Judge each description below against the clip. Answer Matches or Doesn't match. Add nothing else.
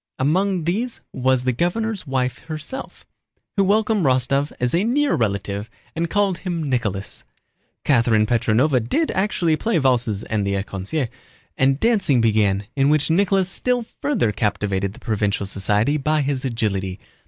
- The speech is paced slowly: Doesn't match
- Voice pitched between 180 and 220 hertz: Doesn't match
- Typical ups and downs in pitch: Doesn't match